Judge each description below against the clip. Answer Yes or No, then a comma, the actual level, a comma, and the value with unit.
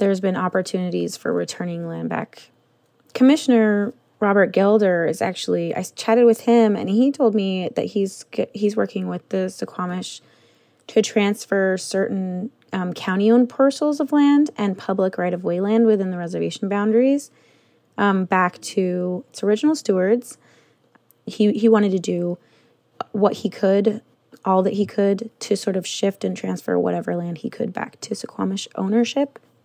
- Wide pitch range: No, average, 3.6 semitones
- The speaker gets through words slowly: No, average, 160 wpm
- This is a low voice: No, high, 200 Hz